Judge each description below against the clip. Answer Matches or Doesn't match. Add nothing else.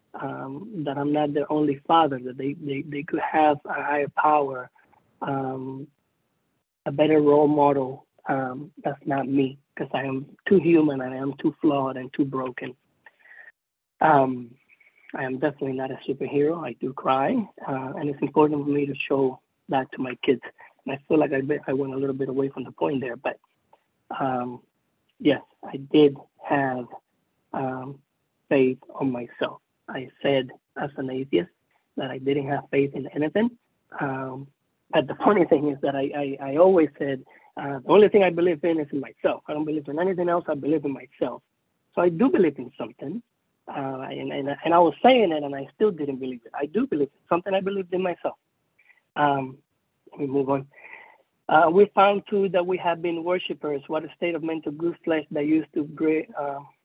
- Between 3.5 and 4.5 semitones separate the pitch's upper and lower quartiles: Doesn't match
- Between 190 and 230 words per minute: Matches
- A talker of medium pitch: Matches